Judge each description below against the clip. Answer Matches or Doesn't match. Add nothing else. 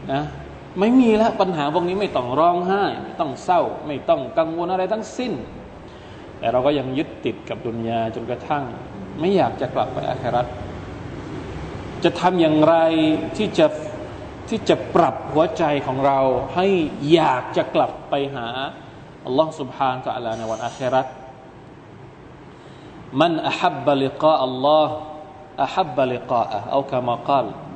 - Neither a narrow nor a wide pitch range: Matches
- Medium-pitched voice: Matches